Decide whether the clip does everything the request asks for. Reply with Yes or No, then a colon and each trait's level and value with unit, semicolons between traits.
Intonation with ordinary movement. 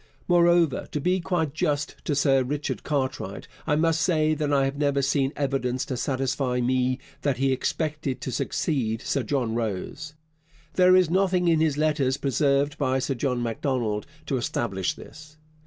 Yes: average, 3.2 semitones